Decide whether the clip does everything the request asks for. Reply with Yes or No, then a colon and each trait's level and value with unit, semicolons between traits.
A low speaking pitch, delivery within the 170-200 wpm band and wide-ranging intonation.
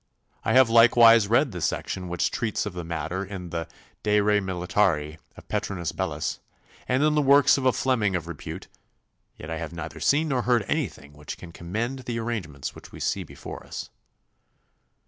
Yes: low, 100 Hz; average, 185 wpm; wide, 5.8 semitones